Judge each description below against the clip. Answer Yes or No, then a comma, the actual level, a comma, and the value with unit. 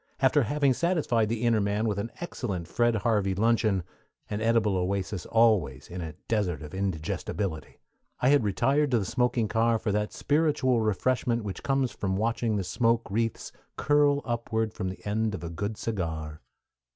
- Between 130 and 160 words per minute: No, average, 170 wpm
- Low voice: Yes, low, 110 Hz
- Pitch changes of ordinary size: Yes, average, 3.5 semitones